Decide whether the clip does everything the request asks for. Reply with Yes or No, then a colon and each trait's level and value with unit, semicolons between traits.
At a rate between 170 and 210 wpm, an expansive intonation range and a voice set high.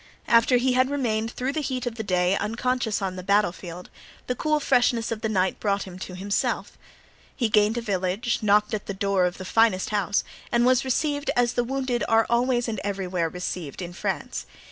No: fast, 205 wpm; average, 4.3 semitones; high, 220 Hz